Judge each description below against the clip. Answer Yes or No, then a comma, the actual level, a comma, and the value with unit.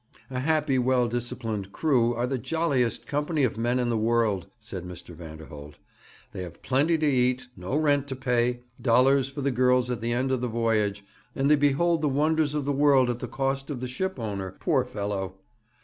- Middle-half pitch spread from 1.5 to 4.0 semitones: Yes, average, 3.7 semitones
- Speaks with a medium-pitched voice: No, low, 125 Hz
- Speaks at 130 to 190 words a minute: No, average, 200 wpm